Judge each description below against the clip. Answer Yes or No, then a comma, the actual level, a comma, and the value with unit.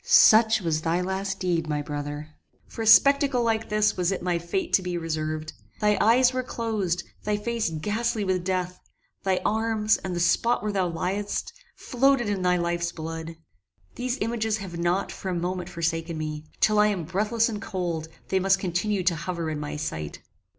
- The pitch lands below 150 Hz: No, medium, 185 Hz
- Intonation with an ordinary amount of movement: Yes, average, 4.1 semitones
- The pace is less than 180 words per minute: No, average, 185 wpm